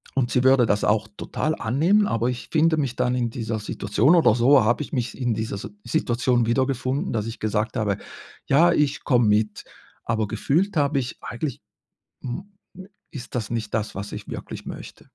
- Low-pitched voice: Yes, low, 120 Hz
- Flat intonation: No, average, 4.0 semitones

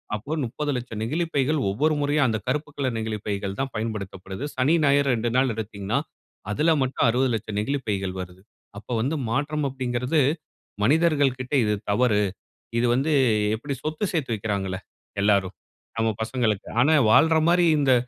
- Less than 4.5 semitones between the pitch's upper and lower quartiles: No, average, 5.3 semitones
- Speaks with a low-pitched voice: Yes, low, 125 Hz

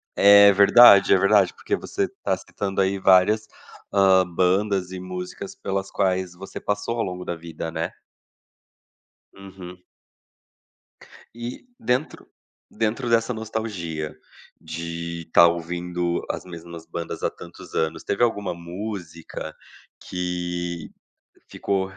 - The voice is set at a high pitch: No, very low, 95 Hz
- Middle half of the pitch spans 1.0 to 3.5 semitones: Yes, average, 2.9 semitones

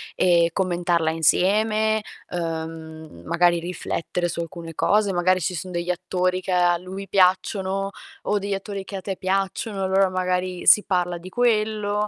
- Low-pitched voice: No, medium, 185 Hz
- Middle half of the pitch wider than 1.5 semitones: Yes, narrow, 2.2 semitones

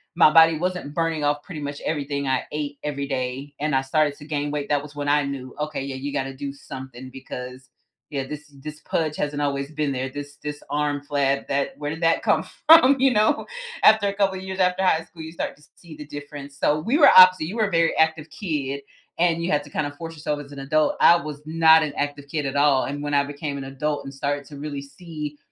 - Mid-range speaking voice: Yes, medium, 145 Hz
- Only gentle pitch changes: Yes, narrow, 2.2 semitones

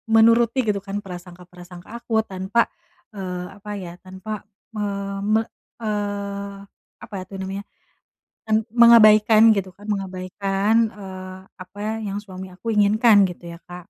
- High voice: Yes, high, 200 Hz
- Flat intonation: Yes, narrow, 2.2 semitones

